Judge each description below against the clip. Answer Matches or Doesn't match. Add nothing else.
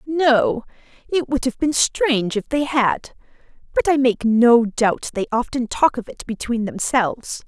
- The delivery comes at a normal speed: Matches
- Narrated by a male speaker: Doesn't match